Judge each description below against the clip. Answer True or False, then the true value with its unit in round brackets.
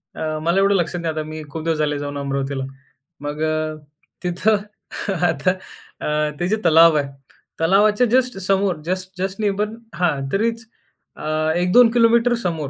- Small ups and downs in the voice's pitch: False (4.4 semitones)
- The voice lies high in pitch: False (175 Hz)